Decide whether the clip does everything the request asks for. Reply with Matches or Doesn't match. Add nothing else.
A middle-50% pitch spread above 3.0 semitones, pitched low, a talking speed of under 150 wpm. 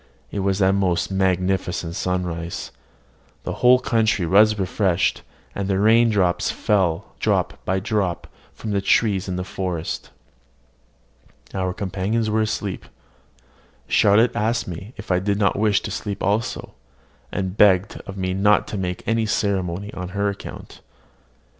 Doesn't match